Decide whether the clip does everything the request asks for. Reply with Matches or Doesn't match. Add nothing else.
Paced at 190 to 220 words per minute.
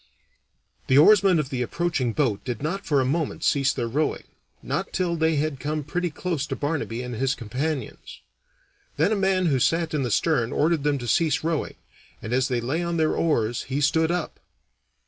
Matches